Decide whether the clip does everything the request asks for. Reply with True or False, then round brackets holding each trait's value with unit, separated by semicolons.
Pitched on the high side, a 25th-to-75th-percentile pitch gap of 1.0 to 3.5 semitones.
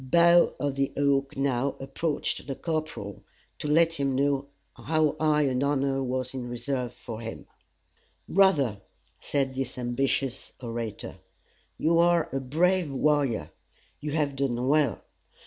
False (140 Hz; 2.9 semitones)